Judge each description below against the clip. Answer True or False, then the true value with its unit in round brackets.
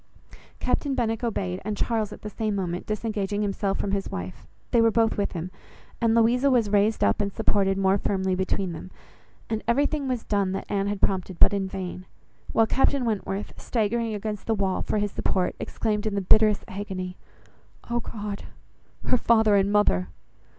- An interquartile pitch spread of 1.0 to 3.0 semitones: True (2.6 semitones)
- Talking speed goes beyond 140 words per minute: True (180 wpm)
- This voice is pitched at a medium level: False (205 Hz)